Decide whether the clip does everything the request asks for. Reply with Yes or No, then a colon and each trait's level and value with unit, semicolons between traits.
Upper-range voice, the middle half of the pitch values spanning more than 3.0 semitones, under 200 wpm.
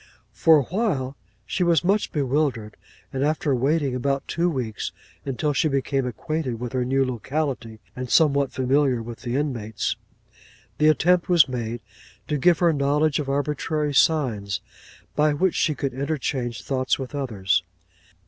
No: medium, 140 Hz; average, 3.4 semitones; average, 150 wpm